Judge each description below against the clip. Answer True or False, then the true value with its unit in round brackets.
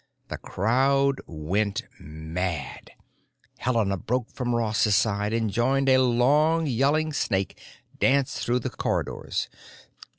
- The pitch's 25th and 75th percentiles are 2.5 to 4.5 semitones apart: False (5.1 semitones)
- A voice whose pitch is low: True (120 Hz)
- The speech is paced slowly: True (110 wpm)